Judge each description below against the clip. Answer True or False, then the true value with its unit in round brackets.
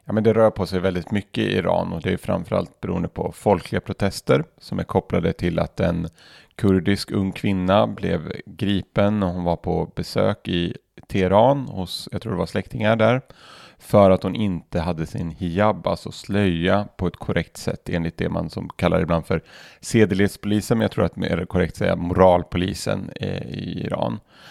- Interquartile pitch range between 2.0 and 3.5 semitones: True (2.7 semitones)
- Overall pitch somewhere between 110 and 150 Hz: False (95 Hz)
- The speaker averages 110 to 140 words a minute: False (185 wpm)